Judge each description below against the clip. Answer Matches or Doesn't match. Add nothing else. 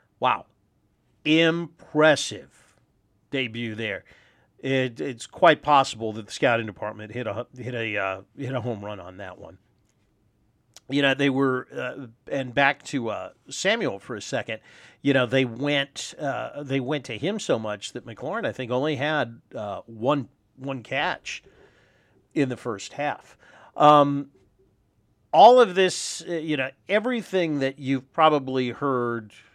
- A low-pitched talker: Matches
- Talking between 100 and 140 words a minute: Doesn't match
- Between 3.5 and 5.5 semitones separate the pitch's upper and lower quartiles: Matches